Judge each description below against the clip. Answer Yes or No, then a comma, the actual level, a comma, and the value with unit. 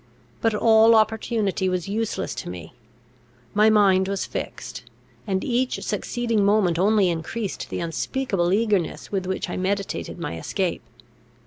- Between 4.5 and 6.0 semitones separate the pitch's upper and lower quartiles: No, average, 3.2 semitones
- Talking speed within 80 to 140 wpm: Yes, slow, 135 wpm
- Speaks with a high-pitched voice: Yes, high, 200 Hz